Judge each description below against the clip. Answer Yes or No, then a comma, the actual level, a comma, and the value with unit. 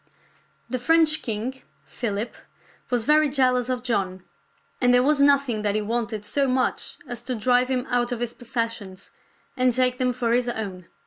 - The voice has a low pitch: No, high, 245 Hz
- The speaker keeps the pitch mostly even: Yes, narrow, 2.1 semitones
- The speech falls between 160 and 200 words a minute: Yes, average, 175 wpm